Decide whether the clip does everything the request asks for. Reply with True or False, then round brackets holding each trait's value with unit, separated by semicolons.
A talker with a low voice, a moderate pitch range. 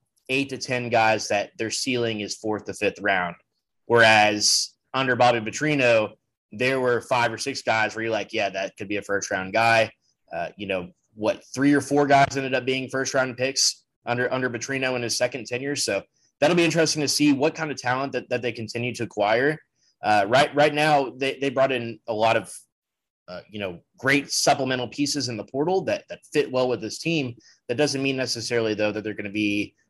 True (125 Hz; 3.8 semitones)